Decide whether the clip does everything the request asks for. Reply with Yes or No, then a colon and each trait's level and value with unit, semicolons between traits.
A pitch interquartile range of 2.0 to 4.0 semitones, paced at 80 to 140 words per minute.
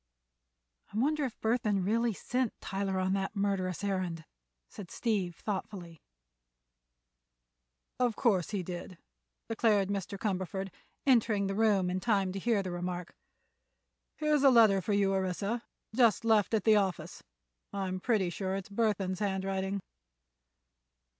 Yes: average, 2.8 semitones; slow, 135 wpm